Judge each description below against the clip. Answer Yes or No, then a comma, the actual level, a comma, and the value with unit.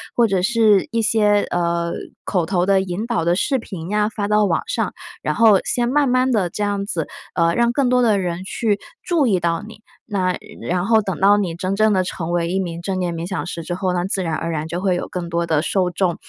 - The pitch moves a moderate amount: Yes, average, 3.5 semitones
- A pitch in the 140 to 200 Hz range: Yes, high, 190 Hz